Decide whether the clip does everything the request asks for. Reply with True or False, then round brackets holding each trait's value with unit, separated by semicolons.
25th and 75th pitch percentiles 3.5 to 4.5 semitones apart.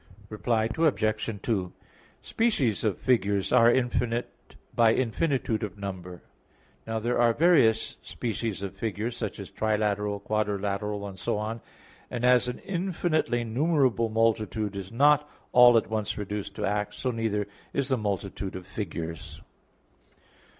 False (3.1 semitones)